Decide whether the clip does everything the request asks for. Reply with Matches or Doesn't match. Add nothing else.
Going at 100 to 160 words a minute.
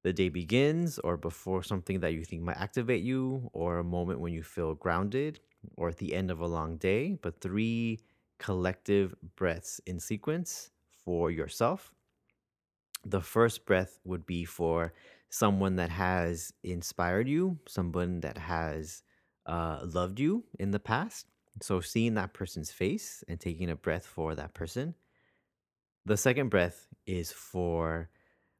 Matches